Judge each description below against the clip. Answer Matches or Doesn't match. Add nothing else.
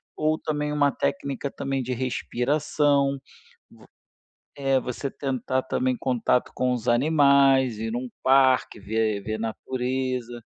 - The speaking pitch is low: Matches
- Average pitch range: Doesn't match